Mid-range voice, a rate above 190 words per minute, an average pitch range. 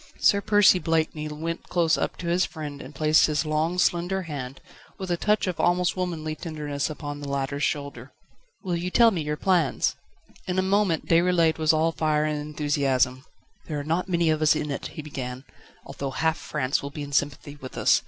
Yes: medium, 155 Hz; average, 200 wpm; average, 3.1 semitones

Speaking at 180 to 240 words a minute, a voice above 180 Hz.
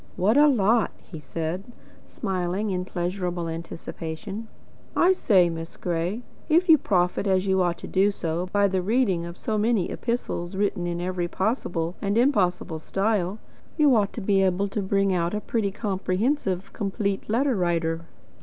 No: average, 160 wpm; high, 190 Hz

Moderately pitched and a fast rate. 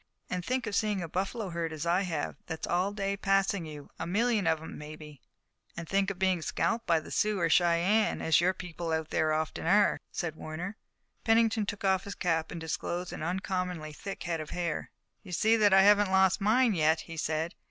Yes: medium, 180 Hz; fast, 210 wpm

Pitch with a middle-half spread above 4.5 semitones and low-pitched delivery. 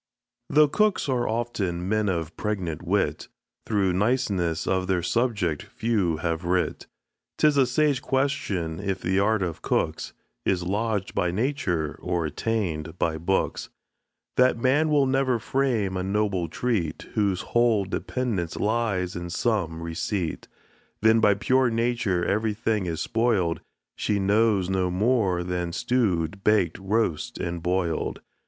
Yes: average, 4.9 semitones; low, 100 Hz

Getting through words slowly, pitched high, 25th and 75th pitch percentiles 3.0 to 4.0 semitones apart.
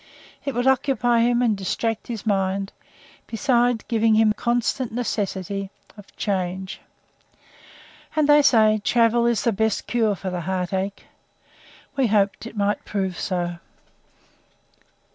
Yes: slow, 130 wpm; high, 220 Hz; average, 3.5 semitones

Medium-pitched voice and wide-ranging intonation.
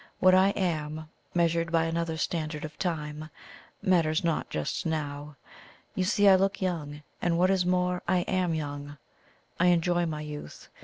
No: medium, 165 Hz; average, 2.8 semitones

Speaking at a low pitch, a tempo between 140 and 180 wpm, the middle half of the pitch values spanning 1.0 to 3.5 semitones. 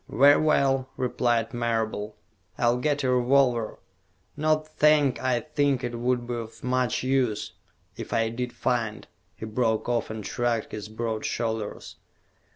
Yes: low, 120 Hz; average, 150 wpm; average, 2.7 semitones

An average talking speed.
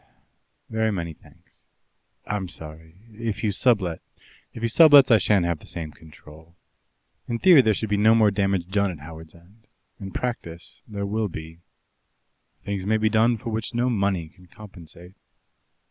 Yes: average, 170 wpm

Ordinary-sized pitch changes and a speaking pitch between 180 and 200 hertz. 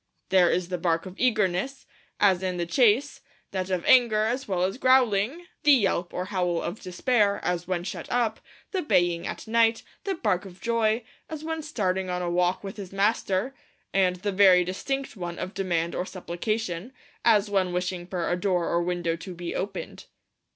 Yes: average, 4.0 semitones; high, 190 Hz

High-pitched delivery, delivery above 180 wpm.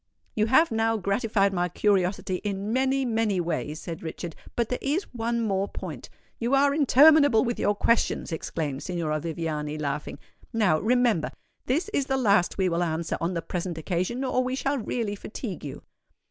No: high, 205 Hz; average, 165 wpm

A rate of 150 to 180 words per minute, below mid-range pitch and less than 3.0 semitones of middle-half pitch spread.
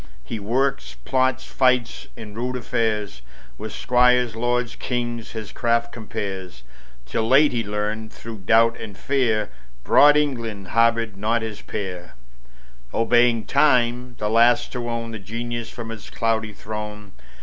No: average, 140 wpm; low, 115 Hz; narrow, 2.4 semitones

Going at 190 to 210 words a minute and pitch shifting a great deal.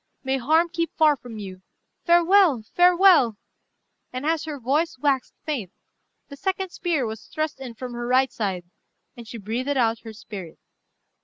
No: average, 160 wpm; wide, 6.0 semitones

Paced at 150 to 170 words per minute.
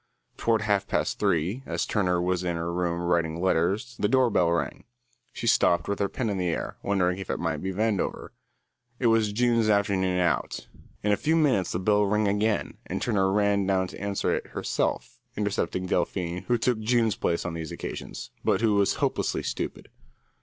No: average, 190 wpm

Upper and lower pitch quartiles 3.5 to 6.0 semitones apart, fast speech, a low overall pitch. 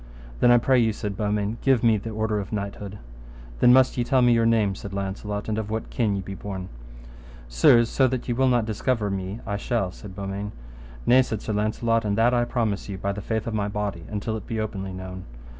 No: average, 2.7 semitones; fast, 230 wpm; low, 105 Hz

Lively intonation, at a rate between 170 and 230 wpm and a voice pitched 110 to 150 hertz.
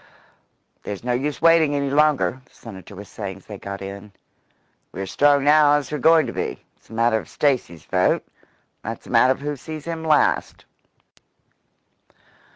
Yes: wide, 6.6 semitones; average, 180 wpm; low, 135 Hz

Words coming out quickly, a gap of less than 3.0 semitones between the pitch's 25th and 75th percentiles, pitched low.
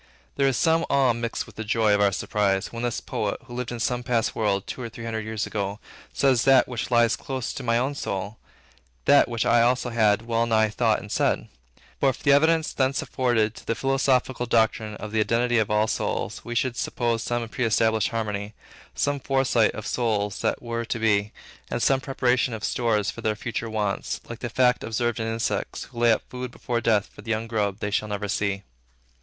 Yes: fast, 210 wpm; narrow, 2.4 semitones; low, 115 Hz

